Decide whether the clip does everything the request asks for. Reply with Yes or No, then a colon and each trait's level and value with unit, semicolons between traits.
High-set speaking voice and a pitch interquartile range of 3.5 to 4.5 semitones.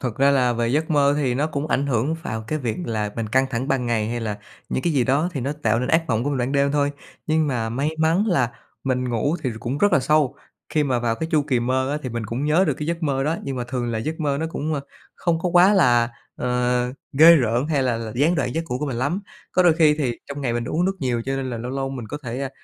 No: low, 135 Hz; average, 4.0 semitones